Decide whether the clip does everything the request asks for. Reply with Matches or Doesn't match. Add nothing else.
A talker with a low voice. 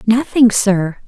Doesn't match